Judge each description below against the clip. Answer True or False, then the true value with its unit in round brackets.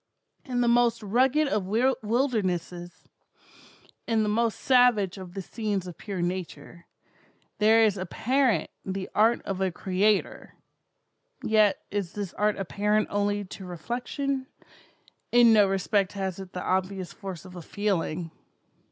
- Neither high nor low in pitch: False (205 Hz)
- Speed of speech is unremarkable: False (130 wpm)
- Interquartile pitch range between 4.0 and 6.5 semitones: False (3.5 semitones)